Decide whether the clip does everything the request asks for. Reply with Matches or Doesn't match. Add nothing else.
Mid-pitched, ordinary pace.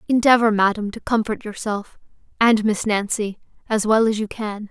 Doesn't match